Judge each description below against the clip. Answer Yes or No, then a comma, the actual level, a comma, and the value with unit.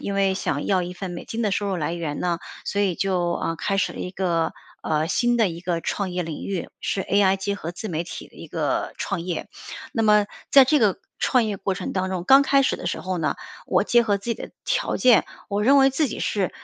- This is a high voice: Yes, high, 195 Hz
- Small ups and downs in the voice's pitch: No, average, 3.5 semitones